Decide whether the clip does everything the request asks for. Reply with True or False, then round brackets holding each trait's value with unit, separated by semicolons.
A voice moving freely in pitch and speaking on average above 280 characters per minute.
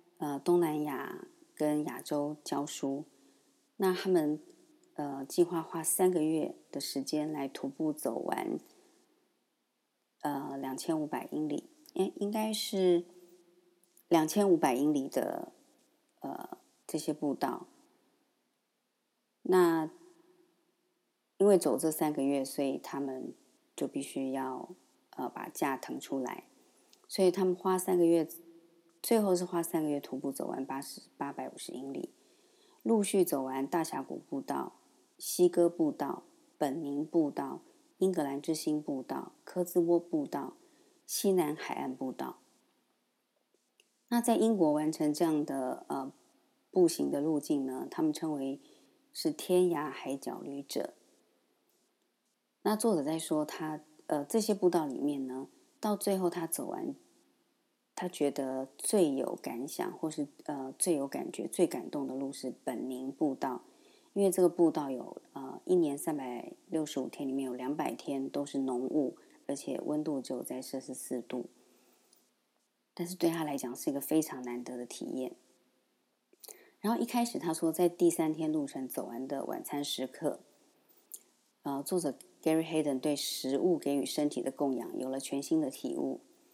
False (7.8 semitones; 215 characters per minute)